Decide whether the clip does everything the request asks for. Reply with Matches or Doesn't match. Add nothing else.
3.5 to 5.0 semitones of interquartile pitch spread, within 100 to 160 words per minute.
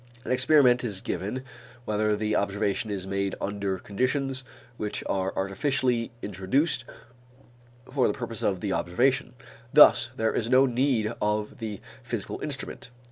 Matches